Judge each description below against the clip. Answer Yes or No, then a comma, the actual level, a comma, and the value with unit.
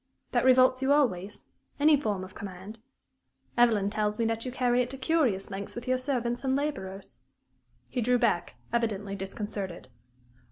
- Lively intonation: No, average, 4.3 semitones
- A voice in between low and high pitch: No, high, 235 Hz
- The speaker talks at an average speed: Yes, average, 160 wpm